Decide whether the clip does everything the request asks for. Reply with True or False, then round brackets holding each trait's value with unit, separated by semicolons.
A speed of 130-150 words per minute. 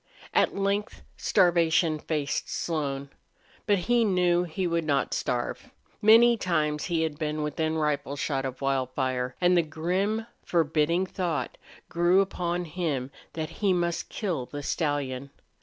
True (140 wpm)